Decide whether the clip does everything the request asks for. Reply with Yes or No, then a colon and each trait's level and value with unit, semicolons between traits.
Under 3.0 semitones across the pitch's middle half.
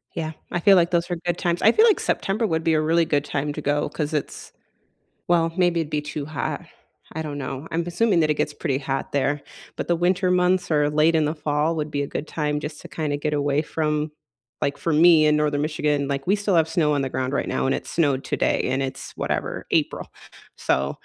Yes: narrow, 2.6 semitones